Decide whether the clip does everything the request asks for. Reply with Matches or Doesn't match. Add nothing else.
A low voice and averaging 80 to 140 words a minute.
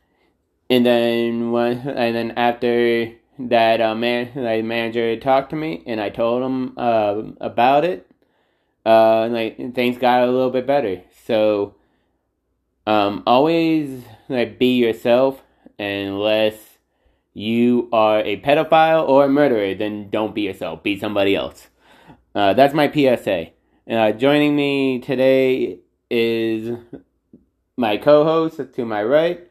Matches